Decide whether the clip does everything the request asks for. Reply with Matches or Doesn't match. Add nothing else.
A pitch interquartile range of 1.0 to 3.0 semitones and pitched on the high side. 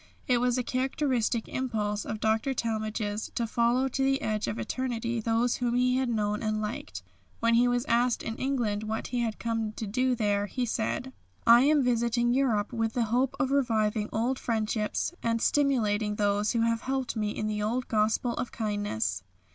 Matches